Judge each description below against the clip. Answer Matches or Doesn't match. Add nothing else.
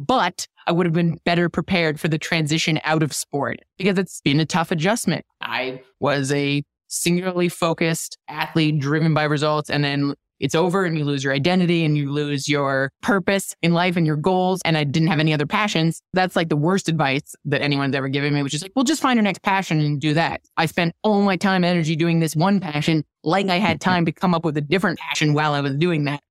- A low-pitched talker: Doesn't match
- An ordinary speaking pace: Doesn't match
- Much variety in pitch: Doesn't match